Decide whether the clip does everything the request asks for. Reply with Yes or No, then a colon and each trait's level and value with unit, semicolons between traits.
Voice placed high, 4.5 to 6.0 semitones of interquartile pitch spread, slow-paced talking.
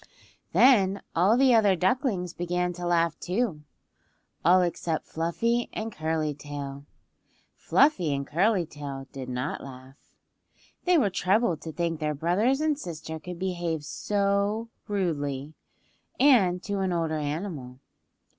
No: medium, 175 Hz; average, 5.0 semitones; slow, 125 wpm